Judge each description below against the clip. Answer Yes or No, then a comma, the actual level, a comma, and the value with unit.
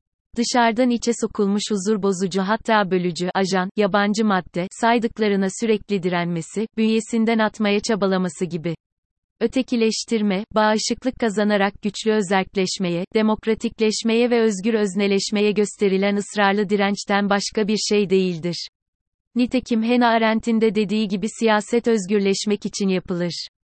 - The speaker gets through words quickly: No, average, 110 wpm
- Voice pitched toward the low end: No, high, 210 Hz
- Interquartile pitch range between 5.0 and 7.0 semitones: No, narrow, 2.4 semitones